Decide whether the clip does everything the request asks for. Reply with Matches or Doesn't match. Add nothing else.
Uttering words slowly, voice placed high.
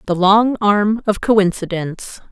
Matches